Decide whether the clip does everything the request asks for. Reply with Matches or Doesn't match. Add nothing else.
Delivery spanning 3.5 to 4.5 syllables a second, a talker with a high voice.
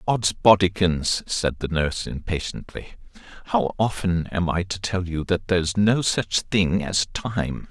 Doesn't match